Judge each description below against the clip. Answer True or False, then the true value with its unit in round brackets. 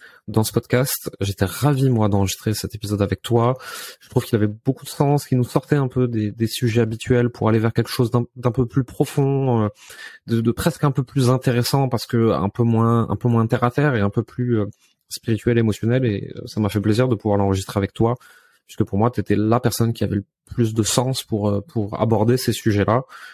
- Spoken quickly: True (235 wpm)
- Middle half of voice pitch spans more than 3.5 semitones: False (3.0 semitones)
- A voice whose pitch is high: False (115 Hz)